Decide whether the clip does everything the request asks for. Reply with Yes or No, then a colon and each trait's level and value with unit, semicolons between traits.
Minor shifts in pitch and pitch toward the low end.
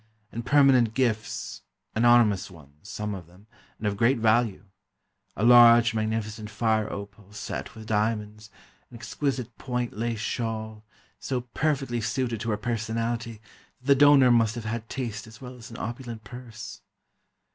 Yes: narrow, 2.2 semitones; low, 115 Hz